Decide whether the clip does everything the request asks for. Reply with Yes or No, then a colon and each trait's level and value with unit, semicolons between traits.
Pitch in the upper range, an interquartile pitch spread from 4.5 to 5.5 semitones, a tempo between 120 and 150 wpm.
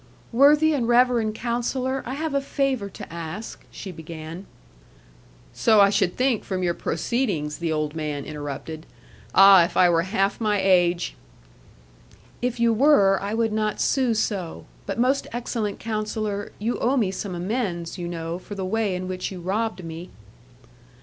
No: high, 200 Hz; average, 5.2 semitones; average, 165 wpm